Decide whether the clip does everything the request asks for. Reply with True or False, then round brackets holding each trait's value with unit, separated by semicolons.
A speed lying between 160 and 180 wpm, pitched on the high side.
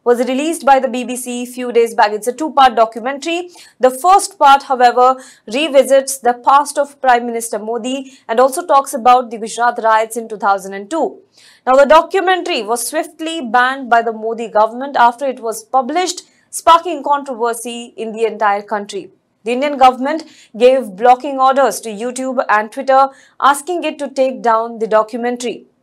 True (165 wpm; 255 Hz)